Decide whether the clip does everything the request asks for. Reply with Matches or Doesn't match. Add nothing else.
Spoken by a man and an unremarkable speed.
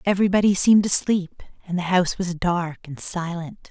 Doesn't match